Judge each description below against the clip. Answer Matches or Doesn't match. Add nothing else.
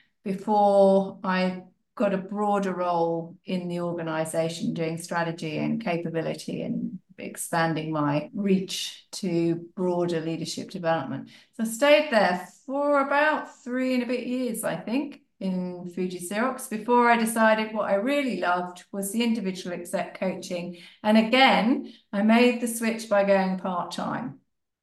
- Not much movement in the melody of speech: Doesn't match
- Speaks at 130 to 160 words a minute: Matches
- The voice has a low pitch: Doesn't match